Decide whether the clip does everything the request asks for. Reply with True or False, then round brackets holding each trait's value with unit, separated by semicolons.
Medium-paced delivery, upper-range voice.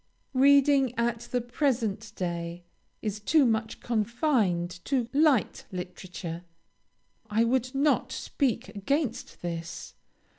False (105 wpm; 230 Hz)